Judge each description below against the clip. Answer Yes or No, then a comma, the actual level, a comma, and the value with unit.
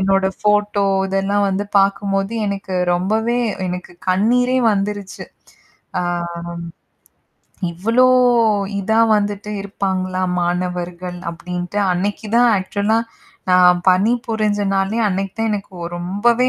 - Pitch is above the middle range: Yes, high, 195 Hz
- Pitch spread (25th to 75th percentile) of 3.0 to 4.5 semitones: No, narrow, 2.4 semitones